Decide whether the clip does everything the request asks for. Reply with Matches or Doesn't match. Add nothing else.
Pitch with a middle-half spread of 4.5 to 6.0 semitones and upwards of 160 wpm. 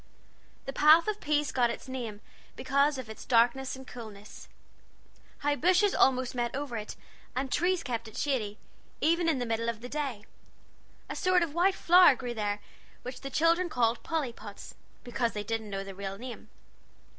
Matches